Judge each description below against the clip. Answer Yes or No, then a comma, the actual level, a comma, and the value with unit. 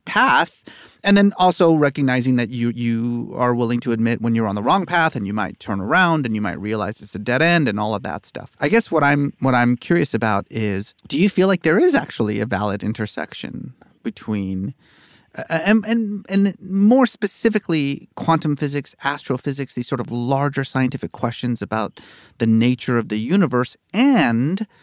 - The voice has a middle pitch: No, low, 130 Hz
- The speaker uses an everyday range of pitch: No, wide, 7.2 semitones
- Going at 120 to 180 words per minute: No, average, 190 wpm